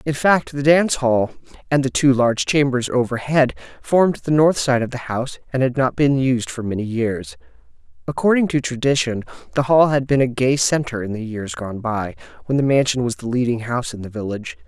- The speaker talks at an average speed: No, fast, 210 wpm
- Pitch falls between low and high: No, low, 125 Hz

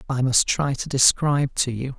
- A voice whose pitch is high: No, low, 135 Hz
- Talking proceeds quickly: Yes, fast, 210 wpm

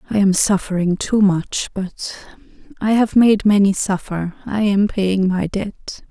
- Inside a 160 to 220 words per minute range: No, average, 145 wpm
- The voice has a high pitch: Yes, high, 200 Hz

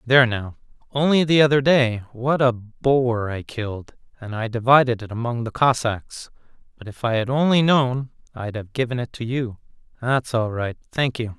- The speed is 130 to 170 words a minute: No, average, 185 wpm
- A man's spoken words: Yes, male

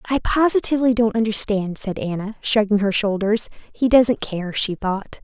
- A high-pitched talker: Yes, high, 215 Hz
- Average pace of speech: Yes, average, 150 wpm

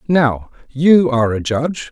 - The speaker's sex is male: Yes, male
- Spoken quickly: No, average, 155 wpm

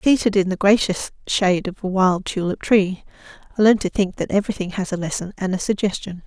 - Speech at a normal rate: No, fast, 210 wpm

